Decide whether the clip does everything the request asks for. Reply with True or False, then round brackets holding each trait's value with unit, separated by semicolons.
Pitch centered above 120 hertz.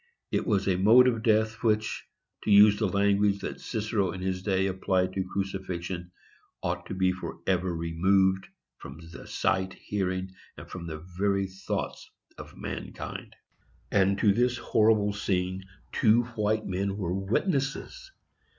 False (95 Hz)